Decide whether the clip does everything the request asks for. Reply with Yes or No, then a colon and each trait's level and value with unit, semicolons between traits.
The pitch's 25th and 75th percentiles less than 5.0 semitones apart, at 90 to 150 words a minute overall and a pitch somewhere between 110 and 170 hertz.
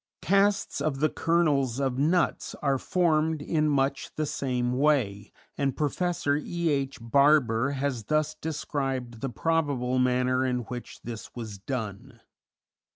Yes: average, 3.6 semitones; slow, 135 wpm; low, 135 Hz